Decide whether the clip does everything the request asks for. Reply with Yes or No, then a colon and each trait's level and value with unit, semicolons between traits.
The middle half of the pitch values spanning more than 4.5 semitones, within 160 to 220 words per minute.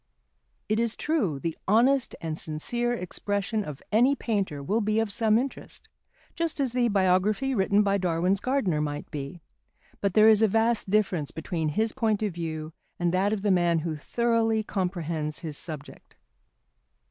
Yes: average, 5.2 semitones; average, 165 wpm